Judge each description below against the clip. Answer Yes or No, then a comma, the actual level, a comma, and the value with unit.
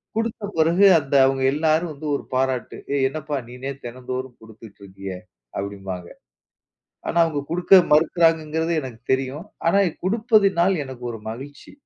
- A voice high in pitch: No, medium, 140 Hz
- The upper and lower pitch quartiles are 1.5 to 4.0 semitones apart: No, average, 5.0 semitones